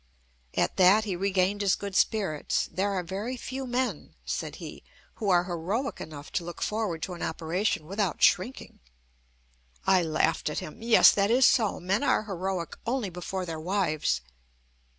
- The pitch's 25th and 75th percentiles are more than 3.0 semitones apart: Yes, average, 3.7 semitones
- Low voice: No, high, 190 Hz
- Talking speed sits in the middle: Yes, average, 165 wpm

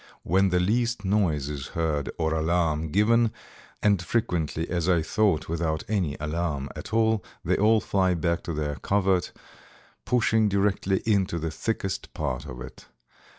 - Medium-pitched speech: No, very low, 90 Hz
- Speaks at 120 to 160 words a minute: Yes, average, 150 wpm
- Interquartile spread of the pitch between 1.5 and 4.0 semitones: No, average, 4.7 semitones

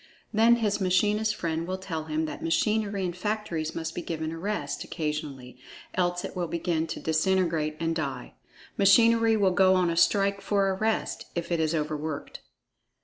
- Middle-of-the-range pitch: Yes, medium, 175 Hz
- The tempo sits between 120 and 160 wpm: No, average, 175 wpm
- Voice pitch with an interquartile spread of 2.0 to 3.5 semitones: No, average, 3.9 semitones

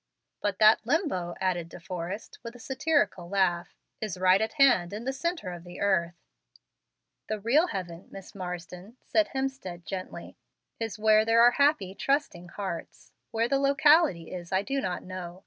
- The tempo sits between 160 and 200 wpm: Yes, average, 165 wpm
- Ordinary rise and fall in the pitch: No, wide, 6.8 semitones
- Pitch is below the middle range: No, high, 200 Hz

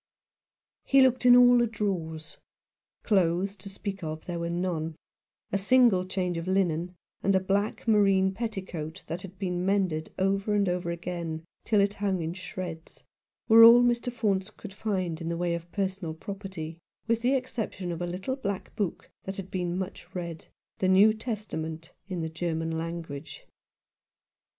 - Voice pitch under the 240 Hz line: Yes, medium, 185 Hz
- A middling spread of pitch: Yes, average, 3.3 semitones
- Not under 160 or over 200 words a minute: Yes, average, 170 wpm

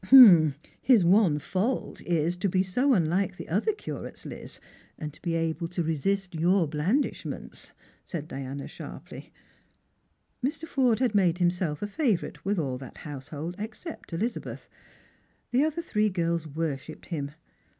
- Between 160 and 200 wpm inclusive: No, average, 140 wpm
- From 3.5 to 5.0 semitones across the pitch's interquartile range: Yes, average, 4.7 semitones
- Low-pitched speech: No, medium, 175 Hz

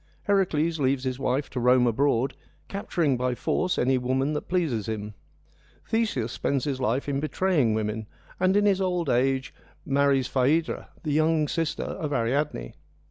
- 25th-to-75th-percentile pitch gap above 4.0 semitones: Yes, average, 4.4 semitones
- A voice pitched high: No, medium, 140 Hz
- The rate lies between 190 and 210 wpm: No, average, 155 wpm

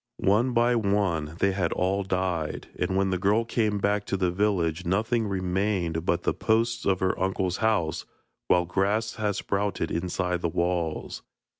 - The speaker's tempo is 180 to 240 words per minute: No, average, 165 wpm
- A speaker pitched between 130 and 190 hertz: No, very low, 95 Hz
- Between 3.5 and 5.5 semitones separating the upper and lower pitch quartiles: No, average, 2.8 semitones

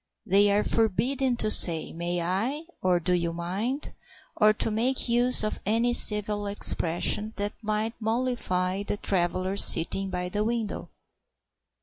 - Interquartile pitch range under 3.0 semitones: No, average, 3.8 semitones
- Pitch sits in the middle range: No, high, 205 Hz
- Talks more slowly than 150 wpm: Yes, average, 140 wpm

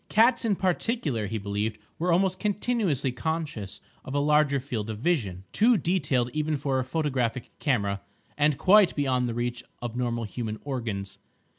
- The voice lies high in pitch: No, low, 135 Hz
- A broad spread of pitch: Yes, wide, 6.2 semitones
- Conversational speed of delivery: Yes, average, 160 wpm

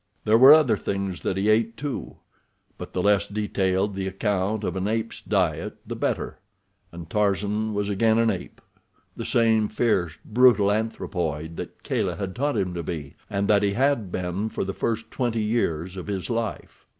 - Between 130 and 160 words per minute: No, average, 175 wpm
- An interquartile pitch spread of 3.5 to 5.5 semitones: No, average, 3.0 semitones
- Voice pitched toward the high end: No, low, 105 Hz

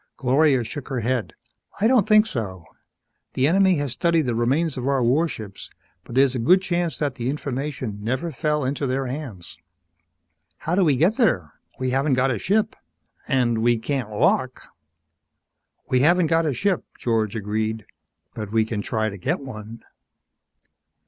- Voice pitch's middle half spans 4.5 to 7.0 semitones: Yes, average, 5.3 semitones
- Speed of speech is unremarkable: Yes, average, 165 wpm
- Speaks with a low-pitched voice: Yes, low, 130 Hz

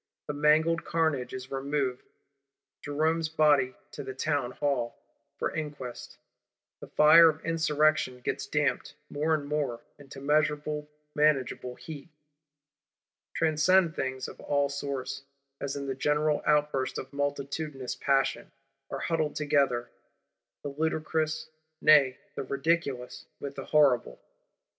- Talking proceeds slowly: Yes, slow, 120 wpm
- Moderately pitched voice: Yes, medium, 145 Hz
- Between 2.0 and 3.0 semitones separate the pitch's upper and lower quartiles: Yes, narrow, 2.4 semitones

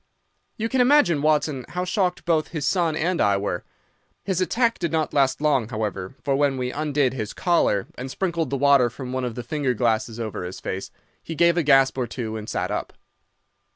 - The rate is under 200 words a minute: No, fast, 205 wpm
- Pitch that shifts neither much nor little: No, wide, 5.7 semitones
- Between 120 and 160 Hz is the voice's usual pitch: Yes, medium, 140 Hz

